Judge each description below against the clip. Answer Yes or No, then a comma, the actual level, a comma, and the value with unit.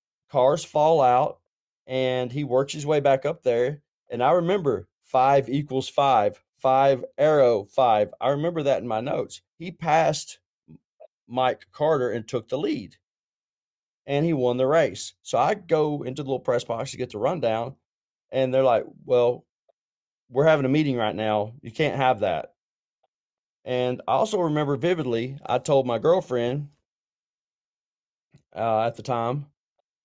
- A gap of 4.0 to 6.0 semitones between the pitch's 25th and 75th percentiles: No, average, 3.4 semitones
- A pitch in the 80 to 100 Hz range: No, low, 130 Hz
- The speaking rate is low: No, average, 155 wpm